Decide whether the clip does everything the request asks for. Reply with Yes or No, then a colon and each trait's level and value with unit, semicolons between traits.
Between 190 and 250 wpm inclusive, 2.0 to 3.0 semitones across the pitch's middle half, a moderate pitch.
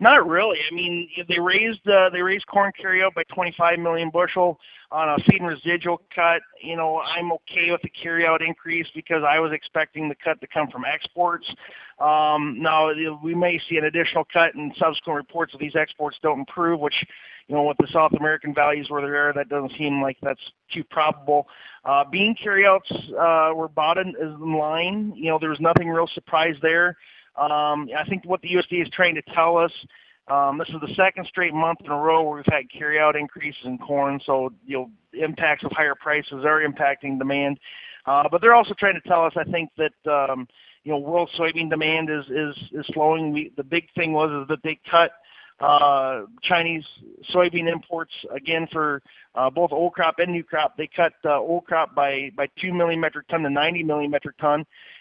Yes: fast, 205 wpm; narrow, 2.5 semitones; medium, 160 Hz